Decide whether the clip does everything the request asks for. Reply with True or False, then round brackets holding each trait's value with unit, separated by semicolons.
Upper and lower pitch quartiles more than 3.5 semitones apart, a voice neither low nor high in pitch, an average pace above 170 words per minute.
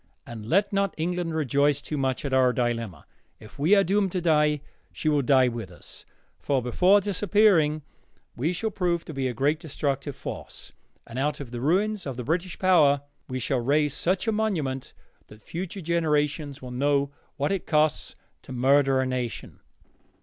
True (4.9 semitones; 145 Hz; 180 wpm)